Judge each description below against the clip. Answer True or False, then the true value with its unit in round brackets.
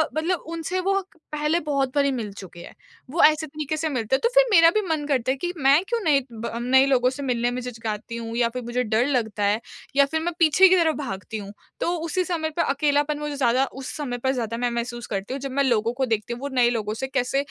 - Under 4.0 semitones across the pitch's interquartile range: False (4.4 semitones)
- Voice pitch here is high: True (265 Hz)